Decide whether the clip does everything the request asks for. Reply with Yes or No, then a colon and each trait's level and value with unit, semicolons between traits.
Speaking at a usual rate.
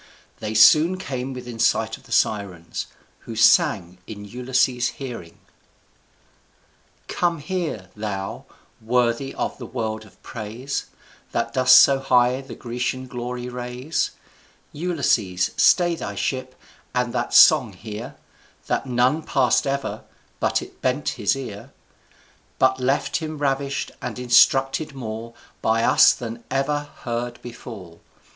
No: slow, 130 wpm